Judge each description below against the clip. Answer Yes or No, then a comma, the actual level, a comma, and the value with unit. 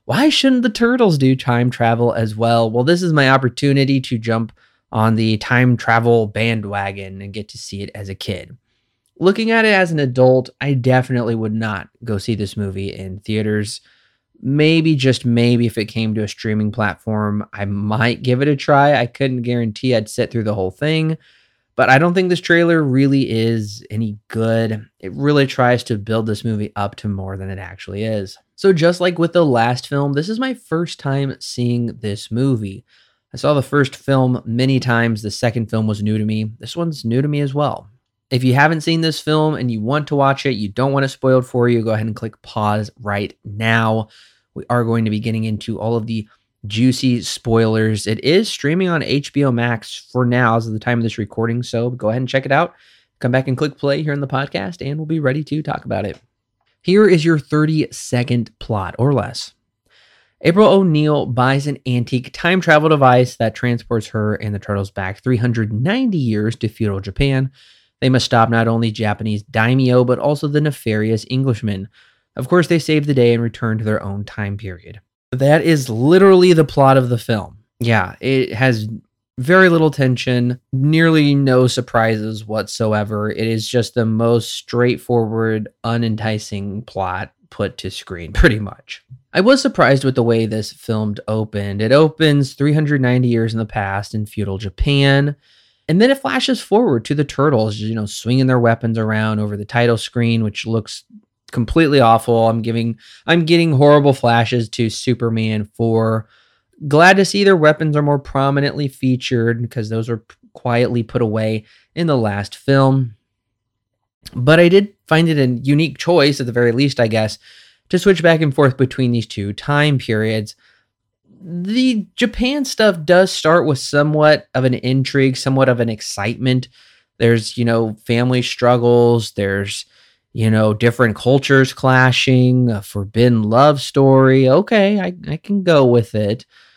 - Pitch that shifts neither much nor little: Yes, average, 4.3 semitones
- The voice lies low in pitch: Yes, low, 120 Hz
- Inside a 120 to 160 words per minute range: No, average, 185 wpm